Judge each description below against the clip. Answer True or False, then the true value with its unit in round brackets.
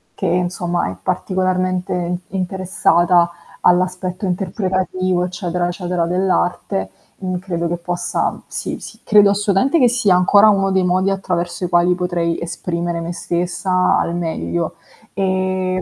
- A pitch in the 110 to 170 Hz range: False (180 Hz)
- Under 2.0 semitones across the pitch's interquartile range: True (1.4 semitones)